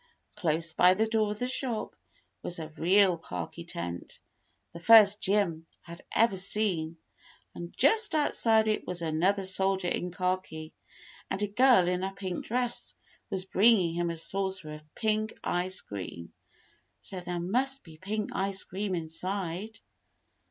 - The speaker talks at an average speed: Yes, average, 150 wpm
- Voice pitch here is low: No, high, 190 Hz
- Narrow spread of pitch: No, average, 4.0 semitones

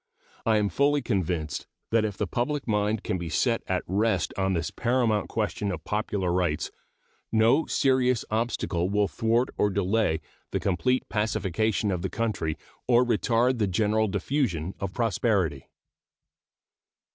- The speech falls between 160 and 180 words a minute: No, average, 145 wpm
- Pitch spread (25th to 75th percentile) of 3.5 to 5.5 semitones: Yes, average, 3.8 semitones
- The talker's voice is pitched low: Yes, low, 105 Hz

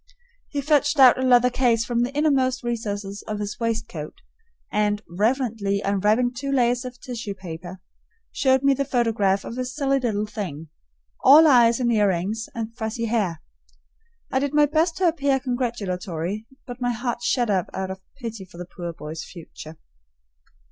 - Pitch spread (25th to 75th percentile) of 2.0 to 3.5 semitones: No, average, 4.3 semitones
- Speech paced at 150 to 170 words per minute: Yes, average, 165 wpm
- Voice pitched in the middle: No, high, 230 Hz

